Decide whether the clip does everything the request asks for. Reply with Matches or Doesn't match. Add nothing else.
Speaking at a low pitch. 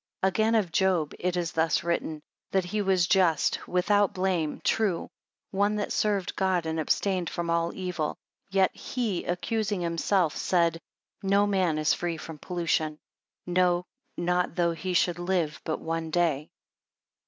Doesn't match